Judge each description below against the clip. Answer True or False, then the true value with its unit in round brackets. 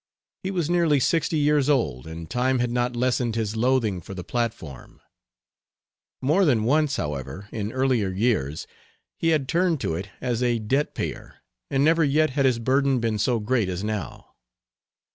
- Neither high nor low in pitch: False (125 Hz)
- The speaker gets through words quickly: False (170 wpm)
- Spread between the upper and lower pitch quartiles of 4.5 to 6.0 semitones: True (5.2 semitones)